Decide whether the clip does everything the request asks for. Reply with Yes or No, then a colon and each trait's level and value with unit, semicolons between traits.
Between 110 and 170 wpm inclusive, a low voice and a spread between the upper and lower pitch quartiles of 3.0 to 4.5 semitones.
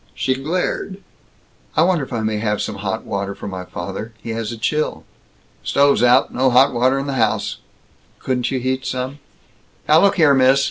No: average, 190 wpm; low, 130 Hz; average, 4.0 semitones